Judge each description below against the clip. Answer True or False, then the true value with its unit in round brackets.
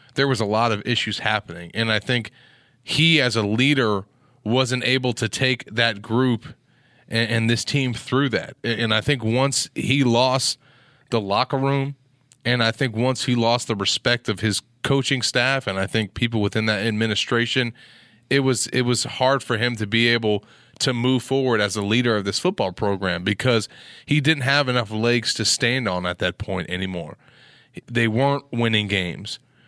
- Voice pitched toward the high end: False (120 Hz)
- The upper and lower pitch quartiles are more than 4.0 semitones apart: False (3.2 semitones)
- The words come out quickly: False (185 wpm)